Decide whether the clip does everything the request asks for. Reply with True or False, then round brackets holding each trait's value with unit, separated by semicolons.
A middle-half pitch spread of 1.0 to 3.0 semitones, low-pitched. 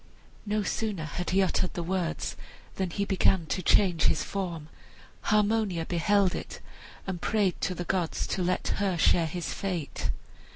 False (2.5 semitones; 185 Hz)